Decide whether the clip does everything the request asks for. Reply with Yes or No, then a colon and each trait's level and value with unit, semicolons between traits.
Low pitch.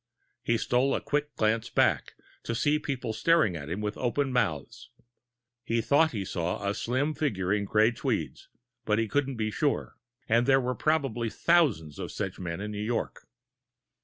Yes: low, 115 Hz